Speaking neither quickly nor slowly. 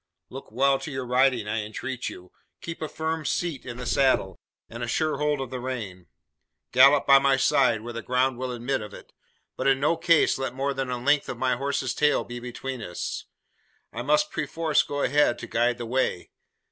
No: fast, 210 wpm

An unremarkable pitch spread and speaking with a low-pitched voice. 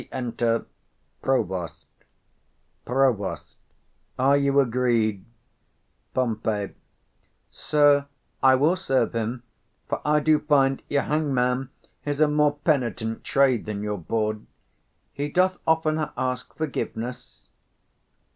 Yes: average, 4.1 semitones; low, 130 Hz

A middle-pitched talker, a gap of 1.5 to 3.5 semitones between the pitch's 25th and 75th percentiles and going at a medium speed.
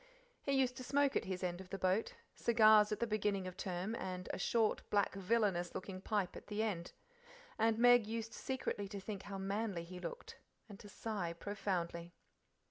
No: high, 205 Hz; average, 3.2 semitones; average, 190 wpm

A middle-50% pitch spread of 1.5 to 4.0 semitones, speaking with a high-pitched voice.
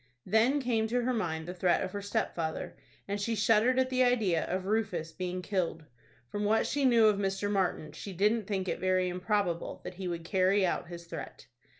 Yes: average, 3.6 semitones; high, 195 Hz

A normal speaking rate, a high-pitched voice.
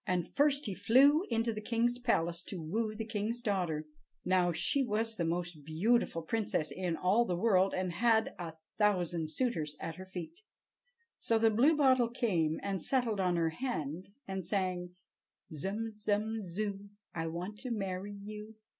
Yes: average, 165 wpm; high, 200 Hz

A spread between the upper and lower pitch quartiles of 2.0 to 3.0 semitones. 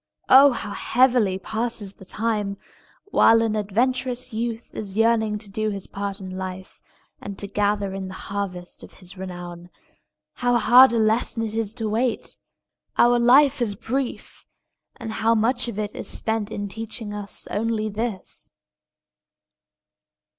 Yes: average, 2.7 semitones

